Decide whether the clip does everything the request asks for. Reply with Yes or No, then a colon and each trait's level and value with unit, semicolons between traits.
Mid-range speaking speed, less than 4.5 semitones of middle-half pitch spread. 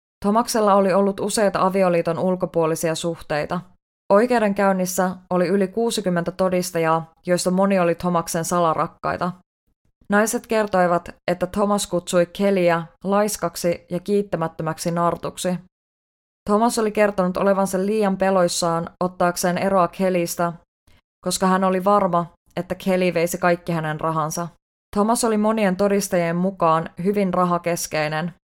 No: slow, 110 wpm; narrow, 2.5 semitones